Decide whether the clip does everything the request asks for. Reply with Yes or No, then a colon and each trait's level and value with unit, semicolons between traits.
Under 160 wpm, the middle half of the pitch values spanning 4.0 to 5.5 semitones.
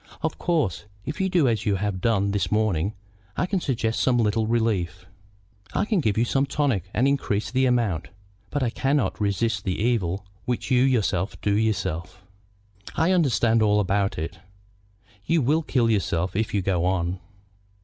No: average, 170 wpm; average, 5.2 semitones